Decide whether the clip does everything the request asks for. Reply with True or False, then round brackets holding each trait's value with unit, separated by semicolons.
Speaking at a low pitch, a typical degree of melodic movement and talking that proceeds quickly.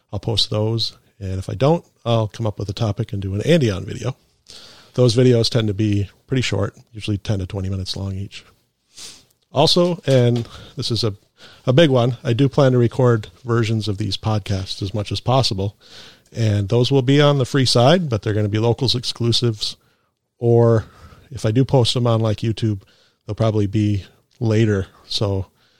False (115 Hz; 3.1 semitones; 190 wpm)